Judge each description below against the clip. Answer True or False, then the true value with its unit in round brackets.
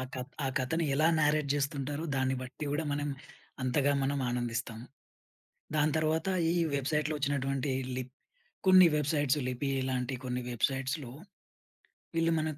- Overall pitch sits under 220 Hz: True (140 Hz)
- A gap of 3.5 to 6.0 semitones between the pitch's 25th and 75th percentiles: False (2.7 semitones)